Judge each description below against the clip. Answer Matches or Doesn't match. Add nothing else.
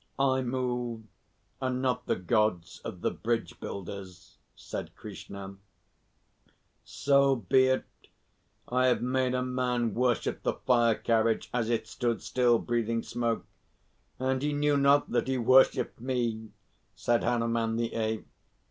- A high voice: Doesn't match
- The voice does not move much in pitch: Matches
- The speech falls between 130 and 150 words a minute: Matches